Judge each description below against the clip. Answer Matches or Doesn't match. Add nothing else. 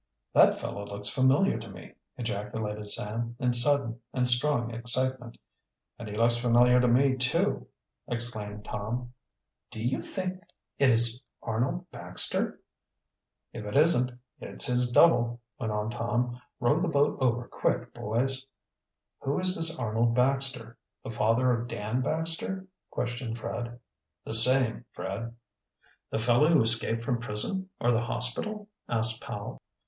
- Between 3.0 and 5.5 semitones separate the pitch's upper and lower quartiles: Doesn't match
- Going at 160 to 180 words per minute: Doesn't match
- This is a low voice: Matches